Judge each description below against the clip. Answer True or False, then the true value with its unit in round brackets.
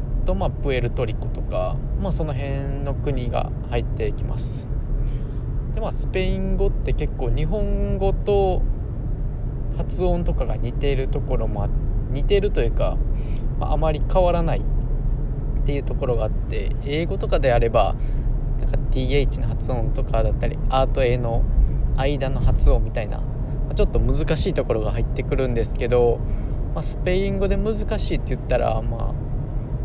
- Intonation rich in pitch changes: False (2.5 semitones)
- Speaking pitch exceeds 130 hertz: False (125 Hz)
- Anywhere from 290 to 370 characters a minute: True (325 characters per minute)